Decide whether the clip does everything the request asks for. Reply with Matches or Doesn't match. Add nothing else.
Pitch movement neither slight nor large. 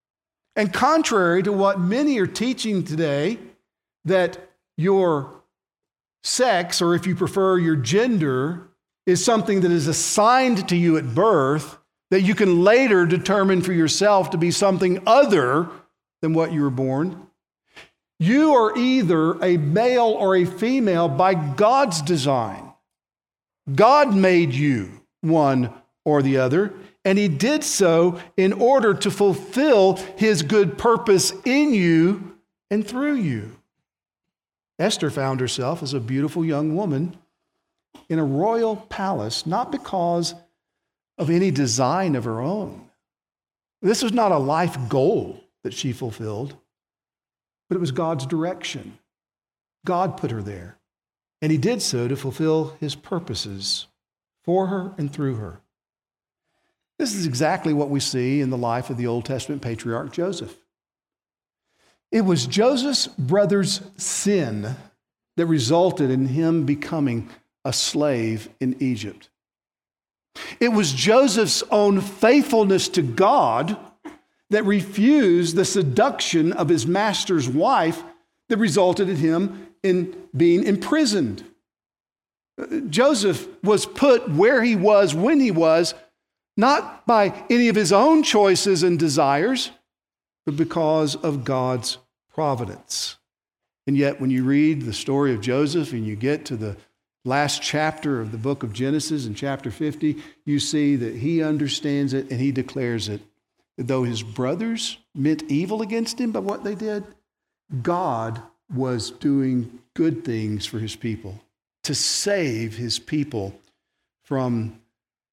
Doesn't match